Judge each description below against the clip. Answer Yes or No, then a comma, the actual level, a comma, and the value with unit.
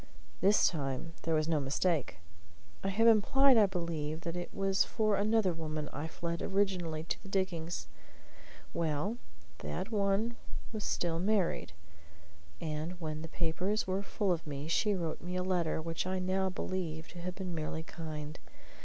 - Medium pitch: Yes, medium, 175 Hz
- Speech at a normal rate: Yes, average, 160 wpm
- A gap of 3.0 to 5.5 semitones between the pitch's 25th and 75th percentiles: Yes, average, 3.5 semitones